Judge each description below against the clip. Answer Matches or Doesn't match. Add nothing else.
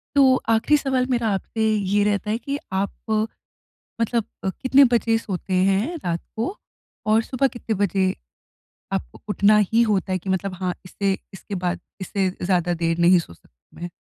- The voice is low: Doesn't match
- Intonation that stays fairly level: Doesn't match